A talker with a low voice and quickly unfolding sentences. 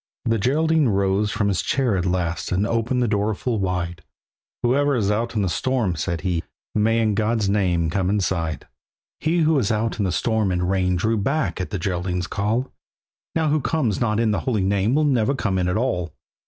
Yes: low, 105 Hz; fast, 210 wpm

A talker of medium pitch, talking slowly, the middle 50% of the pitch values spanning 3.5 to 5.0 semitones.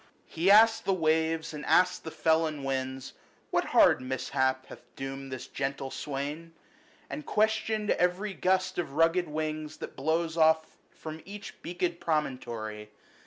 No: medium, 160 Hz; average, 145 wpm; average, 4.6 semitones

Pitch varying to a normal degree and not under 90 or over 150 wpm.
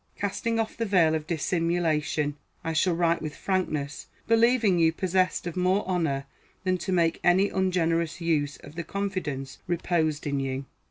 No: average, 3.2 semitones; average, 160 wpm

